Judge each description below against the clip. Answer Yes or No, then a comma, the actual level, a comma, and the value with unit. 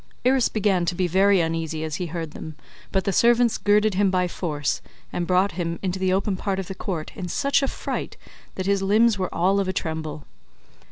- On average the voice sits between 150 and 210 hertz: Yes, medium, 185 Hz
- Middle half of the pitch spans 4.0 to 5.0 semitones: No, average, 3.0 semitones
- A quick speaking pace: Yes, fast, 215 wpm